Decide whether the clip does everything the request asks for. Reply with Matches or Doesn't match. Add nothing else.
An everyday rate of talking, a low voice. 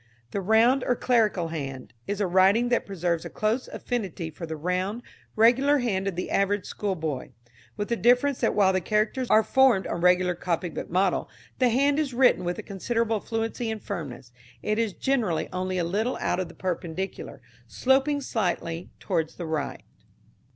Doesn't match